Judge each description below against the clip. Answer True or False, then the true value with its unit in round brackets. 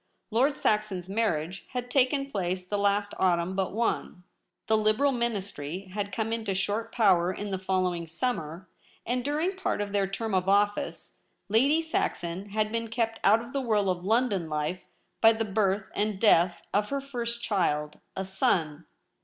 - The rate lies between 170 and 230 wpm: True (175 wpm)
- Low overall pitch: False (205 Hz)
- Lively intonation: False (3.7 semitones)